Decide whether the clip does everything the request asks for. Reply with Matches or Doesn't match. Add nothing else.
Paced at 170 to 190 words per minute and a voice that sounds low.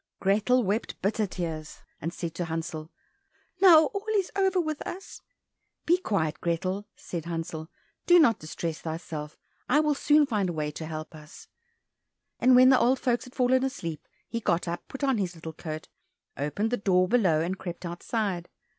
Doesn't match